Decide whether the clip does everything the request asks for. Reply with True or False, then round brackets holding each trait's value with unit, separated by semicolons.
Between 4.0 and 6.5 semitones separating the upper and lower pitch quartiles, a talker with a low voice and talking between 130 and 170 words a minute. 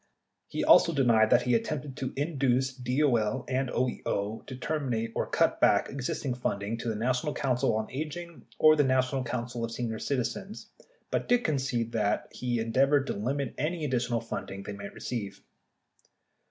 False (3.3 semitones; 125 Hz; 165 wpm)